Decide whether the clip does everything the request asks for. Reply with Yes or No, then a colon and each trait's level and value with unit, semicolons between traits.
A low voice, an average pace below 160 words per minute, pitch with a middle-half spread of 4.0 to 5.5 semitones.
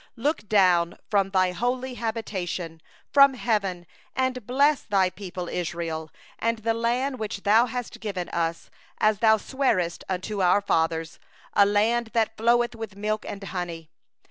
No: high, 205 Hz; average, 145 wpm; average, 4.6 semitones